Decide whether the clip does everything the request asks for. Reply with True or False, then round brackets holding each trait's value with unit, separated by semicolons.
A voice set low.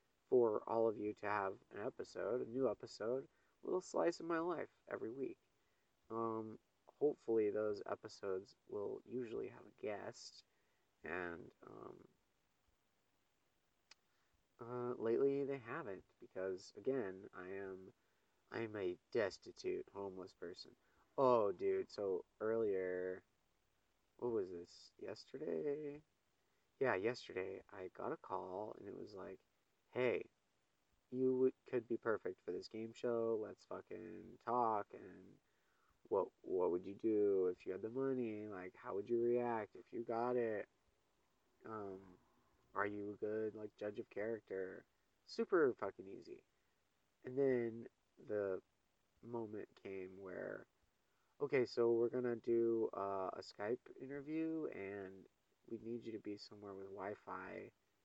True (115 Hz)